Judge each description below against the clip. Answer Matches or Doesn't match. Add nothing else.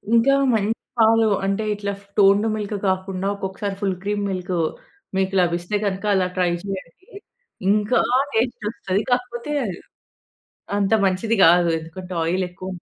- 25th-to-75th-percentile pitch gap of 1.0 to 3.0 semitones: Matches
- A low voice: Doesn't match